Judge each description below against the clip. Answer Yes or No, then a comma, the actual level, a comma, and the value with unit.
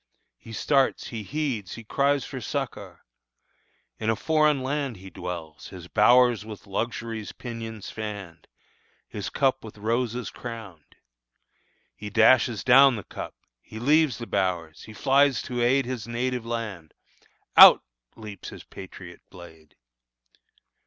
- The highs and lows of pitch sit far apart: No, average, 3.9 semitones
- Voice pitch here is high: No, low, 115 Hz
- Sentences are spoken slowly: Yes, slow, 130 wpm